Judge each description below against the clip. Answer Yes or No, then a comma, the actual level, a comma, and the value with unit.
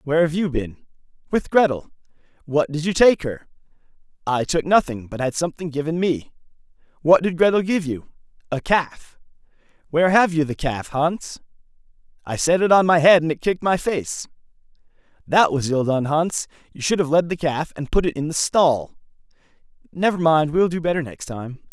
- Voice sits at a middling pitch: Yes, medium, 160 Hz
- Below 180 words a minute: No, average, 185 wpm